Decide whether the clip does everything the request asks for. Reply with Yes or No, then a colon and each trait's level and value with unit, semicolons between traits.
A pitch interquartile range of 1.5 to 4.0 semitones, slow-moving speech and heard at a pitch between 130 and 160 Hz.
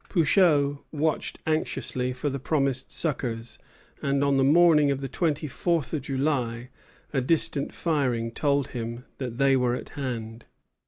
No: average, 3.3 semitones; average, 150 wpm; medium, 140 Hz